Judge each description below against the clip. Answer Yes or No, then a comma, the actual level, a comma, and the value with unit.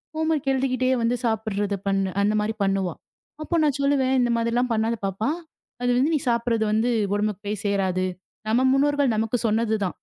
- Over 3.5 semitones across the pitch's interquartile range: Yes, average, 3.9 semitones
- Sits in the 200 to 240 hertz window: Yes, high, 230 Hz